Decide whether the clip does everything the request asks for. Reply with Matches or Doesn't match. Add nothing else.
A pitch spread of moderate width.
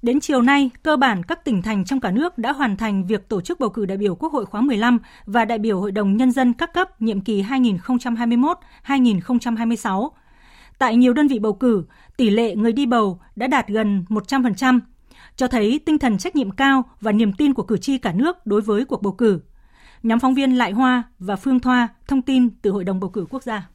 Matches